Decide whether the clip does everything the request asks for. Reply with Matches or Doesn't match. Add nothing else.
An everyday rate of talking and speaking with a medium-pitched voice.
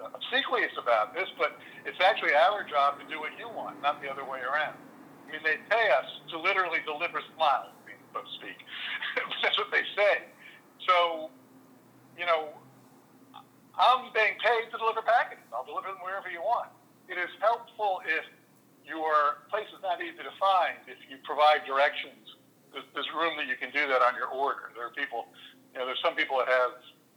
Matches